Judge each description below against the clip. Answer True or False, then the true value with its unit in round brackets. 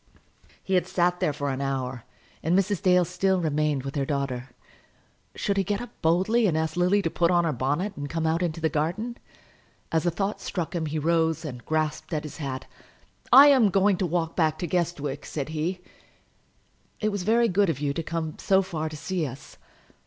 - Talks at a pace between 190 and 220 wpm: True (205 wpm)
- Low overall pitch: False (165 Hz)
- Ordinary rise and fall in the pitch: True (3.6 semitones)